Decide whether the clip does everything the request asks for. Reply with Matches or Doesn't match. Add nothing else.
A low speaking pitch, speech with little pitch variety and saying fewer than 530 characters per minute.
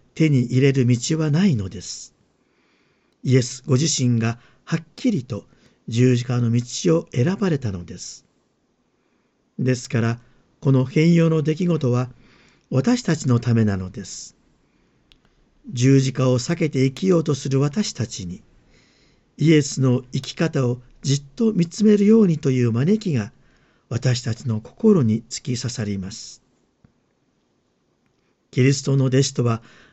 Doesn't match